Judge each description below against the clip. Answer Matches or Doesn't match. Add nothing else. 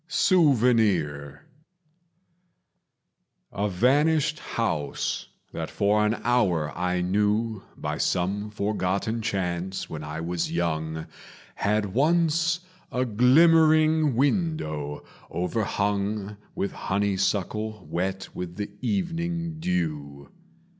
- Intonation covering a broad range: Matches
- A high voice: Doesn't match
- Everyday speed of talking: Doesn't match